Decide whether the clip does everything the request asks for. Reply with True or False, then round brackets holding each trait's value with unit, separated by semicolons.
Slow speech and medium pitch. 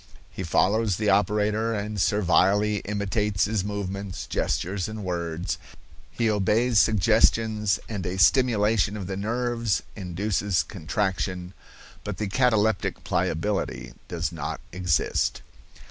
False (115 wpm; 105 Hz)